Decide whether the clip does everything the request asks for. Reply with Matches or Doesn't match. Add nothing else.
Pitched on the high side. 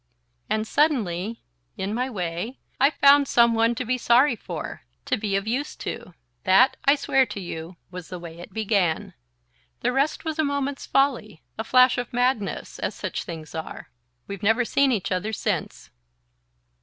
Matches